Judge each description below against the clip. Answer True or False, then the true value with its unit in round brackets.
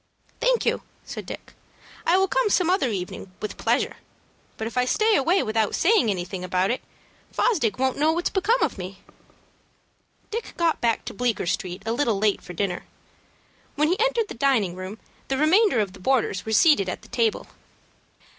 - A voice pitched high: True (245 Hz)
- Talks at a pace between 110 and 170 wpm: False (185 wpm)